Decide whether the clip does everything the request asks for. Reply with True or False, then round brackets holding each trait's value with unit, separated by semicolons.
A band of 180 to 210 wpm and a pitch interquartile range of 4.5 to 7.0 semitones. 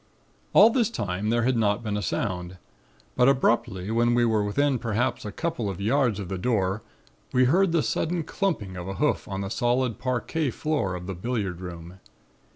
True (190 wpm; 5.1 semitones)